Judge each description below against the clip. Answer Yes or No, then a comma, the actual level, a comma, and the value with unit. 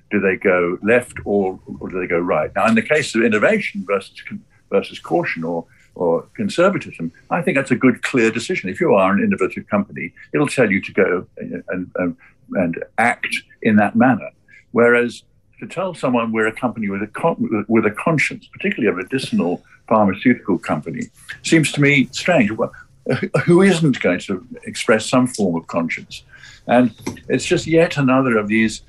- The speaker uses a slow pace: No, average, 175 wpm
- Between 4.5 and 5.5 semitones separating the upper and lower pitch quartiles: Yes, average, 5.2 semitones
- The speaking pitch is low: Yes, low, 120 Hz